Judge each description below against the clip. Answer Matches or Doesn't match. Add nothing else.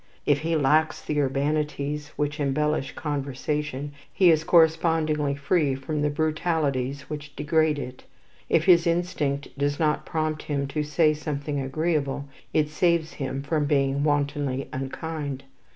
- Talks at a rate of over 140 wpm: Doesn't match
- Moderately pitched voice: Matches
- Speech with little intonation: Matches